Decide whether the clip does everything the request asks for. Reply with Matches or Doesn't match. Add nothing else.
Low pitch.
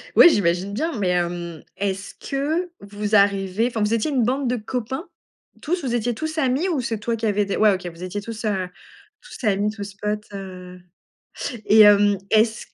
Doesn't match